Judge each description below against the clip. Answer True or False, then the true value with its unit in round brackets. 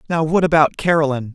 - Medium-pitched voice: True (155 Hz)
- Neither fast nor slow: True (180 wpm)